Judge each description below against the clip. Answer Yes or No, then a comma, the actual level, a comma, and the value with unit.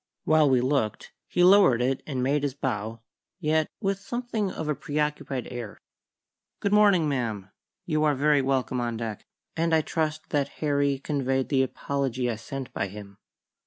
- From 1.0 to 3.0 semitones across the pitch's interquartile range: No, average, 3.8 semitones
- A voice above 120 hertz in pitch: Yes, medium, 140 Hz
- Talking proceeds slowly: No, average, 165 wpm